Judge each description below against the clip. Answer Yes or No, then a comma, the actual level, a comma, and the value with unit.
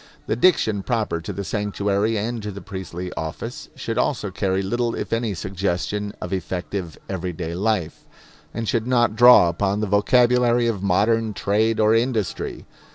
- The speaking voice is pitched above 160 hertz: No, low, 105 Hz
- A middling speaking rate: Yes, average, 160 wpm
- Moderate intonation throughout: Yes, average, 3.3 semitones